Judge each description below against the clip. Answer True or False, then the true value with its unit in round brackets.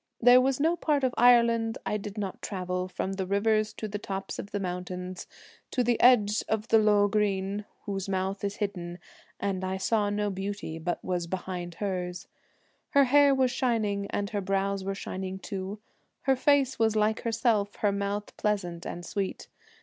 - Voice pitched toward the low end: False (205 Hz)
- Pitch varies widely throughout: False (2.9 semitones)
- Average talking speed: True (175 wpm)